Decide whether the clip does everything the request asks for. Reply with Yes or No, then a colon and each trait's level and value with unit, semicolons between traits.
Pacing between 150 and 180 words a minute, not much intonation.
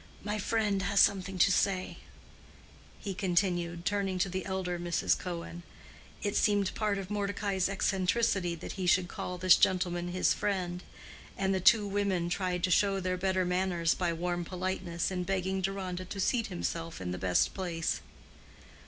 Yes: average, 160 wpm; narrow, 1.9 semitones